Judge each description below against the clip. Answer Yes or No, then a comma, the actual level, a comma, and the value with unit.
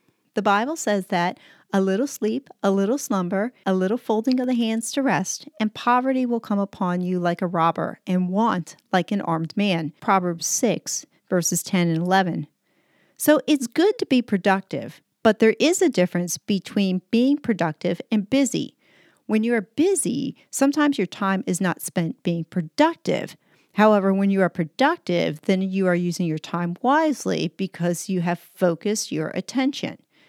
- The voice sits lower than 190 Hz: No, high, 195 Hz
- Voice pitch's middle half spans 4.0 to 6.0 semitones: Yes, average, 5.3 semitones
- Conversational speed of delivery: Yes, average, 170 wpm